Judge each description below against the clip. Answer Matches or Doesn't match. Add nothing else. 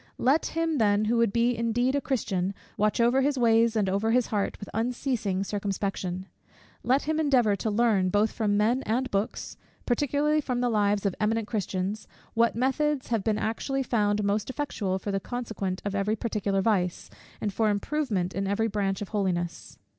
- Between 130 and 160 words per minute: Doesn't match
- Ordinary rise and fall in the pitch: Matches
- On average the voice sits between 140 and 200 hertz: Doesn't match